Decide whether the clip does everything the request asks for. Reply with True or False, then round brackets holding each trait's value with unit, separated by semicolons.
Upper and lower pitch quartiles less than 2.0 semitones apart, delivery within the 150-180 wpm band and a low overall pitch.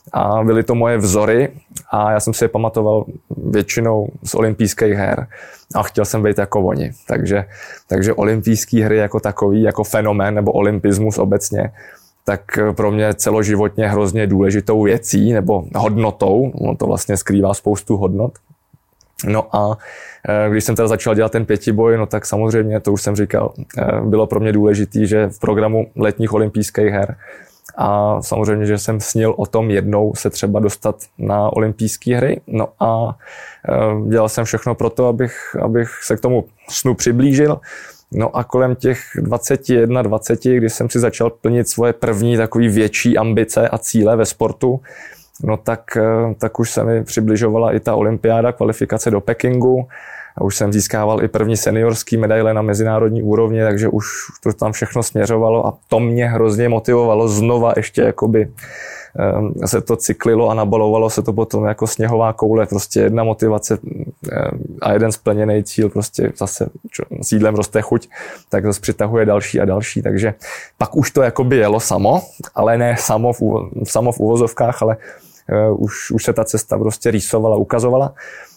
True (1.4 semitones; 160 wpm; 110 Hz)